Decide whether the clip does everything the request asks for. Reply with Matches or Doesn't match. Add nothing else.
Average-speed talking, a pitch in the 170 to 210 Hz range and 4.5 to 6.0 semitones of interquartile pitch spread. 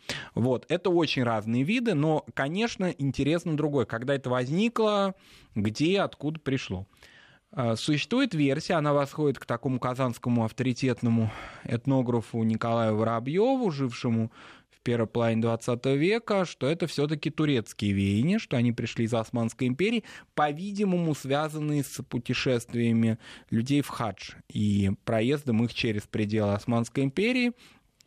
Doesn't match